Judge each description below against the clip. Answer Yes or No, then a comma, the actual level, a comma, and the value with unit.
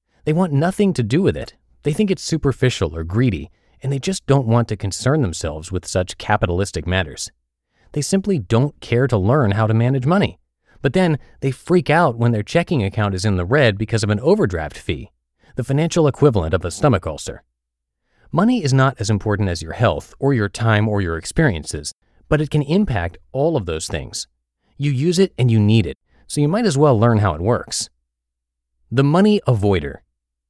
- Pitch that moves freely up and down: Yes, wide, 7.9 semitones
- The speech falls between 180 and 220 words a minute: Yes, average, 200 wpm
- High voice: No, low, 115 Hz